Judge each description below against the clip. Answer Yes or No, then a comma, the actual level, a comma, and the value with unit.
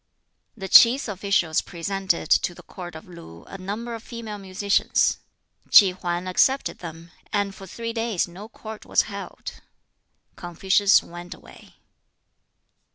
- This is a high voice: Yes, high, 195 Hz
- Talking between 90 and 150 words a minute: Yes, slow, 135 wpm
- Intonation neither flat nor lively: Yes, average, 3.4 semitones